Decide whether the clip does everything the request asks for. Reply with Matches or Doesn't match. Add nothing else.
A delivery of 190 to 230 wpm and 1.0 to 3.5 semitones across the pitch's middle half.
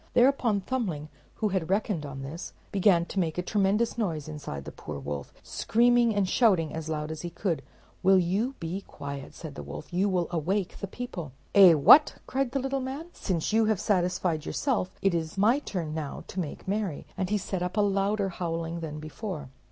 Doesn't match